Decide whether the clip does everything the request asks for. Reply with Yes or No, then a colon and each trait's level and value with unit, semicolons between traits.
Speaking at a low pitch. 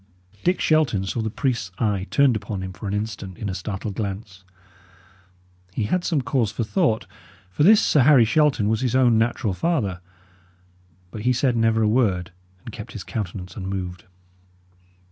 Yes: low, 110 Hz